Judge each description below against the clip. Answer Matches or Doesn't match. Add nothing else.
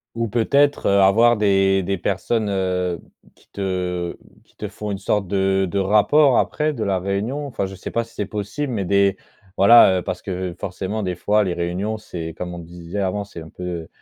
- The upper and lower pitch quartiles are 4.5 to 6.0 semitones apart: Doesn't match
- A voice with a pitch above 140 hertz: Doesn't match